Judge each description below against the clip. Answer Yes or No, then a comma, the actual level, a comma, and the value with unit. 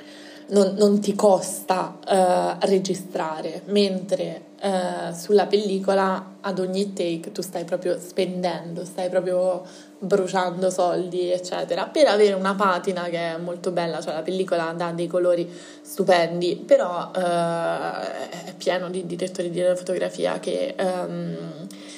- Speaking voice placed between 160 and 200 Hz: Yes, medium, 185 Hz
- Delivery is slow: No, average, 130 wpm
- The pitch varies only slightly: Yes, narrow, 1.8 semitones